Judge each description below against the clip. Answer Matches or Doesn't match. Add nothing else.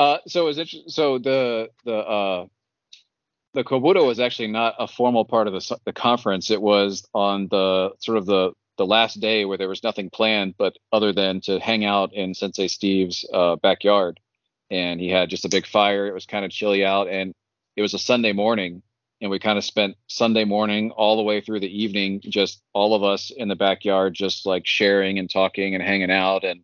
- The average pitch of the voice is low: Matches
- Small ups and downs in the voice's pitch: Matches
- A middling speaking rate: Doesn't match